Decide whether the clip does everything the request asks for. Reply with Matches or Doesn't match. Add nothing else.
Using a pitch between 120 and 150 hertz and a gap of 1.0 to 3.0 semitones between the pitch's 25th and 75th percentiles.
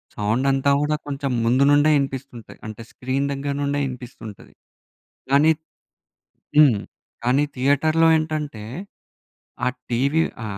Matches